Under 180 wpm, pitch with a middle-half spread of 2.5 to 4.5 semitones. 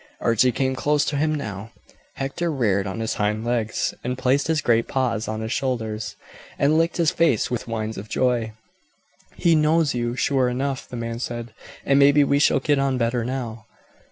No: average, 185 wpm; average, 3.8 semitones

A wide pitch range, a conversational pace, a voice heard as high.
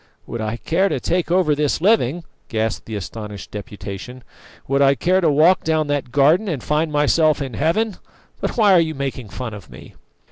No: wide, 6.1 semitones; average, 190 wpm; medium, 145 Hz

